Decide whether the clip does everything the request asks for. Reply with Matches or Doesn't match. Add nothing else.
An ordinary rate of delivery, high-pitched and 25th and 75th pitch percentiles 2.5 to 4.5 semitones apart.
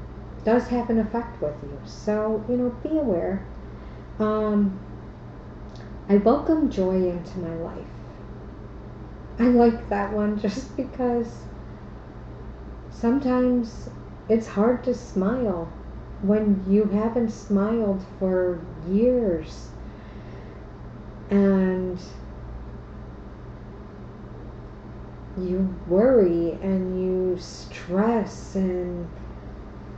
Doesn't match